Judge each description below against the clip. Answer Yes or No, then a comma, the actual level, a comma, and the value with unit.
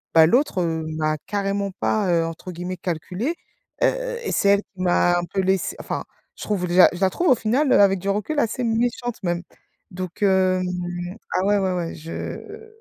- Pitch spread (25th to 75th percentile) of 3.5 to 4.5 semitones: Yes, average, 3.8 semitones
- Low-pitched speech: No, high, 190 Hz